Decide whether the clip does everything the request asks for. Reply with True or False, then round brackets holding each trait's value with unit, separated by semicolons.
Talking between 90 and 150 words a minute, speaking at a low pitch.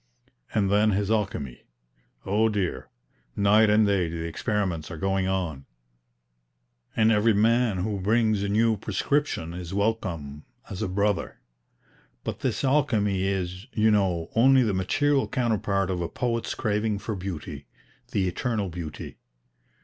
True (140 wpm; 100 Hz)